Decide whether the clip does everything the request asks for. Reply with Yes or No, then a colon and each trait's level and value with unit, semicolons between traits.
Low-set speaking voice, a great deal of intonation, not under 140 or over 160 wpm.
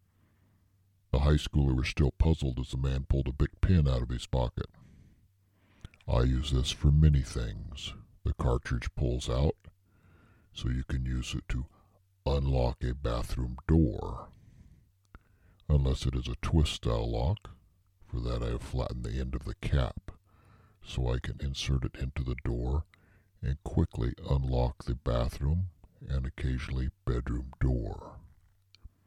Yes: very low, 75 Hz; wide, 6.8 semitones; average, 145 wpm